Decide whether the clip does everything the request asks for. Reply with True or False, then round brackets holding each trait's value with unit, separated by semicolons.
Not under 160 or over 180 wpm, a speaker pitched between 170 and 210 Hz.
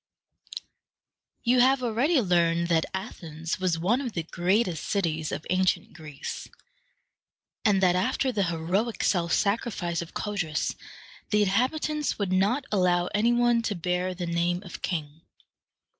False (140 wpm; 185 Hz)